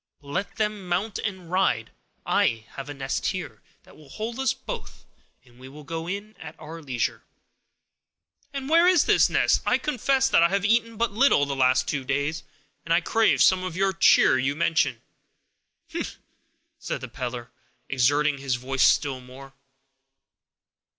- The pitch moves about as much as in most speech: No, wide, 7.8 semitones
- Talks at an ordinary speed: Yes, average, 170 wpm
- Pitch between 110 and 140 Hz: No, medium, 165 Hz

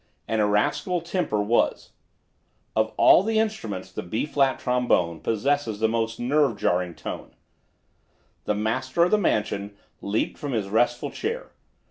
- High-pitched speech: No, low, 115 Hz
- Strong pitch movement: Yes, wide, 5.8 semitones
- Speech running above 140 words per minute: No, slow, 135 wpm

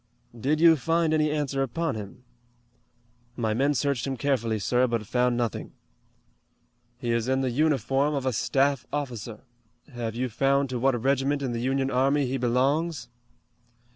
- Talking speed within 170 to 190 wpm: No, average, 160 wpm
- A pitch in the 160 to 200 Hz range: No, low, 130 Hz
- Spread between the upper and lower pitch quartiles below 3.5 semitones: Yes, average, 2.8 semitones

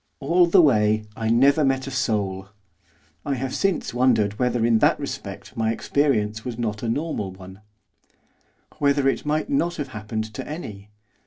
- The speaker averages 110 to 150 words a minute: No, average, 165 wpm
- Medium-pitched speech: No, low, 120 Hz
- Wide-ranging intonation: No, average, 4.9 semitones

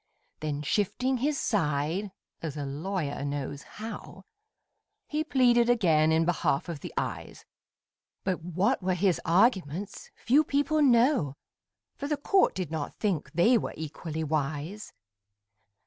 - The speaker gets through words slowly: Yes, slow, 130 wpm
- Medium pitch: Yes, medium, 180 Hz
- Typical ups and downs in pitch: No, wide, 7.7 semitones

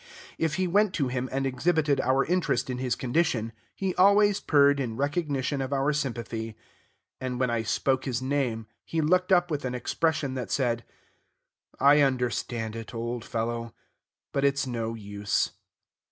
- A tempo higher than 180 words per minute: No, average, 160 wpm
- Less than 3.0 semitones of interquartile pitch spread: No, average, 4.0 semitones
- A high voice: No, low, 130 Hz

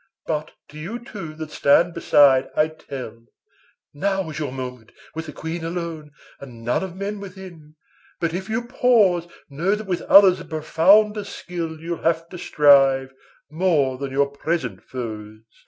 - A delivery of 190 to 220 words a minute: No, average, 165 wpm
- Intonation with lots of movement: No, average, 4.8 semitones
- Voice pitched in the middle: Yes, medium, 160 Hz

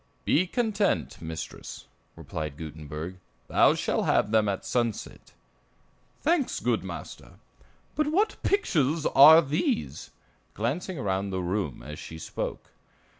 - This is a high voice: No, low, 110 Hz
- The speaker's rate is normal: No, slow, 120 wpm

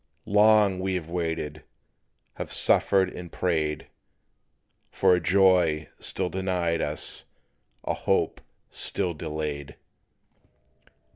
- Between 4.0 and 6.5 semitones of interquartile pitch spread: No, average, 3.2 semitones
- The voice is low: Yes, very low, 90 Hz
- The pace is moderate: No, slow, 95 wpm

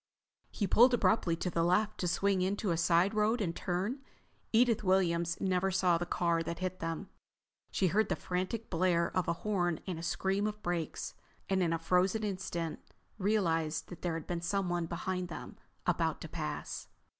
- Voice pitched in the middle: Yes, medium, 180 Hz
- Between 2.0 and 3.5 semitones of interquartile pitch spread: Yes, average, 2.8 semitones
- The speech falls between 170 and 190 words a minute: Yes, average, 180 wpm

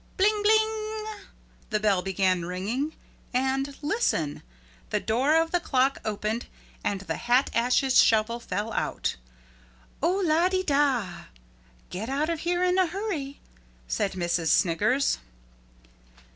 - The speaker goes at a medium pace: No, slow, 130 wpm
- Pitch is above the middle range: Yes, very high, 265 Hz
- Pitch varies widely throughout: Yes, wide, 8.6 semitones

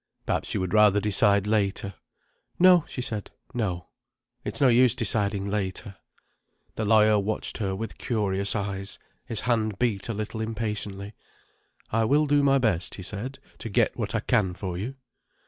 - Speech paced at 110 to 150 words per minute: No, average, 165 wpm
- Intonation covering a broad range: No, average, 2.7 semitones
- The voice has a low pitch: Yes, low, 105 Hz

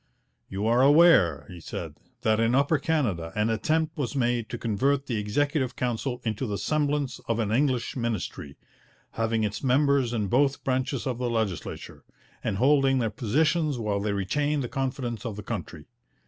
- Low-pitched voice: Yes, low, 120 Hz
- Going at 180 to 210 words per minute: No, average, 170 wpm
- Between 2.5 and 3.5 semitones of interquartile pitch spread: No, average, 4.4 semitones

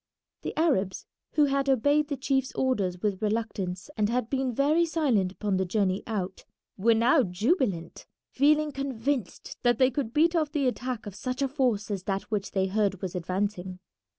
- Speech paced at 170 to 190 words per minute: Yes, average, 180 wpm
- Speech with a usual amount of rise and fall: No, wide, 5.9 semitones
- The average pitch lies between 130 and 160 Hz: No, high, 230 Hz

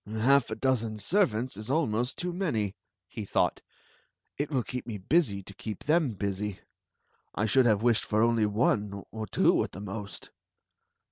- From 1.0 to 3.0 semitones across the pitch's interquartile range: No, average, 4.0 semitones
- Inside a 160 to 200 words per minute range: Yes, average, 175 wpm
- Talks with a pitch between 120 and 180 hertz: No, low, 110 Hz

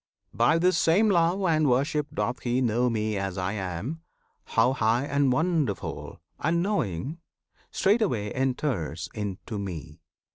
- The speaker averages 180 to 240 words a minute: No, slow, 135 wpm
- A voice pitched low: Yes, low, 125 Hz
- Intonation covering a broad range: Yes, wide, 8.1 semitones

